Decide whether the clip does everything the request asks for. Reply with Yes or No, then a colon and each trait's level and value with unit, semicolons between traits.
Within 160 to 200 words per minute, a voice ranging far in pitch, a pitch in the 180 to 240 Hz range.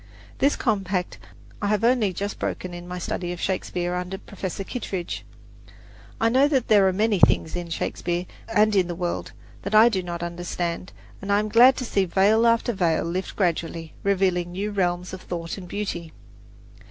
No: average, 175 wpm; average, 3.0 semitones; high, 190 Hz